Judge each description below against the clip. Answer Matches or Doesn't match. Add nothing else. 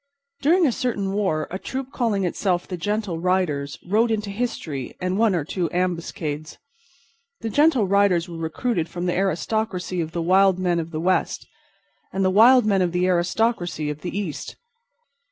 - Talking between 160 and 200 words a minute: Matches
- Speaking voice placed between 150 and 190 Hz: Matches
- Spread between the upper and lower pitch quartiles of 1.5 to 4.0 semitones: Matches